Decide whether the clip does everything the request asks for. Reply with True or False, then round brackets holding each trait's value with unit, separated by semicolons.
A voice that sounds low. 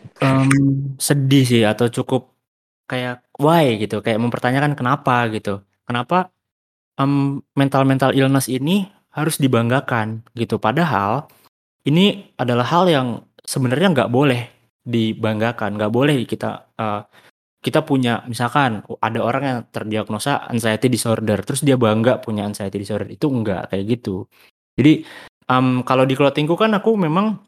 True (125 Hz)